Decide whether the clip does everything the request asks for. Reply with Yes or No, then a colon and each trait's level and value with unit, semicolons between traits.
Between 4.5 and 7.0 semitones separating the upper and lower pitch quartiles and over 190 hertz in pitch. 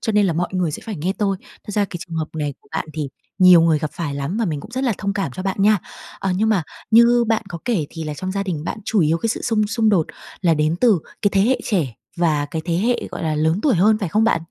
No: average, 4.9 semitones; medium, 185 Hz